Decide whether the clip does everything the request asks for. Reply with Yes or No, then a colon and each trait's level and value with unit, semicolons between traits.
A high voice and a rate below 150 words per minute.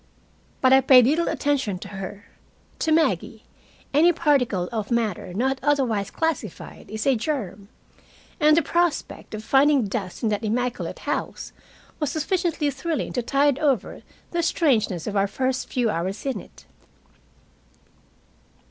Yes: very high, 255 Hz; average, 140 wpm